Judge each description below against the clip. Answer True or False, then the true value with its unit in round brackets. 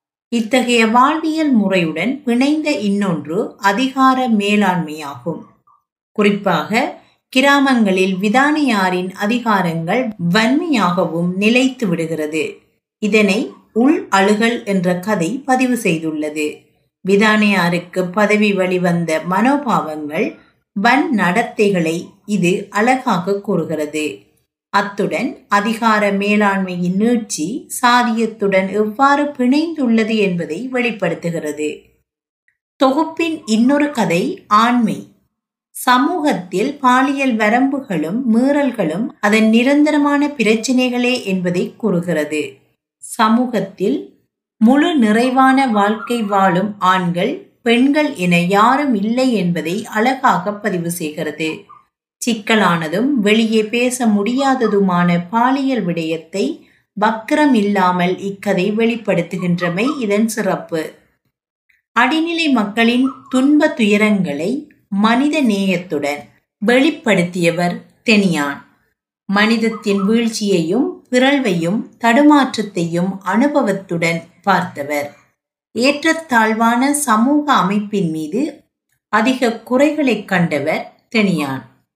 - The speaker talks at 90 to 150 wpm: False (75 wpm)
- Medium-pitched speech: False (215 Hz)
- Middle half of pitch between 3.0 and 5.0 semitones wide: False (5.5 semitones)